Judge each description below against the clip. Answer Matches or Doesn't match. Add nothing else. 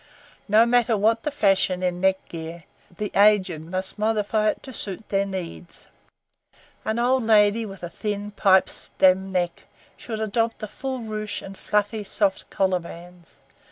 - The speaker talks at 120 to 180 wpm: Matches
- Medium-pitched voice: Doesn't match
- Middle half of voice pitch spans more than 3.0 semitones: Doesn't match